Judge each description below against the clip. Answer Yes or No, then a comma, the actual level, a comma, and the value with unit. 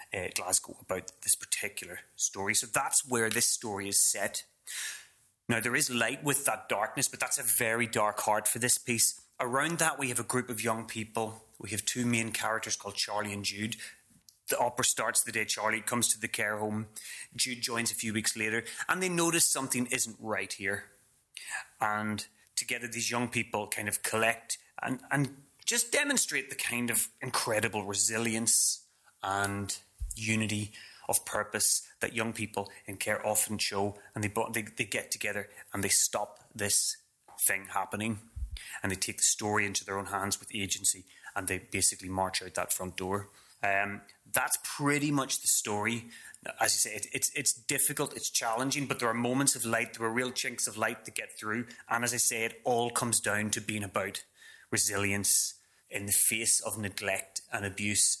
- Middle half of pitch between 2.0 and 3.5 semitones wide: Yes, average, 2.8 semitones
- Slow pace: No, average, 185 wpm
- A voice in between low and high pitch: No, low, 110 Hz